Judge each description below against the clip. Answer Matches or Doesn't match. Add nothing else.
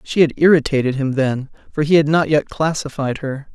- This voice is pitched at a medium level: Matches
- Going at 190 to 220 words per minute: Matches